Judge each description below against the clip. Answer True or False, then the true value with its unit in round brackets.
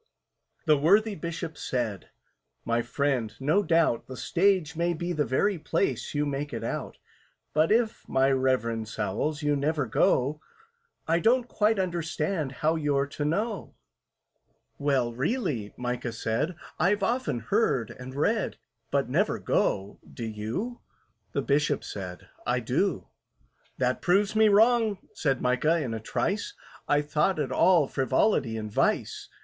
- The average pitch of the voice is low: False (150 Hz)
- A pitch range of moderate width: False (6.4 semitones)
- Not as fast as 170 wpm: True (140 wpm)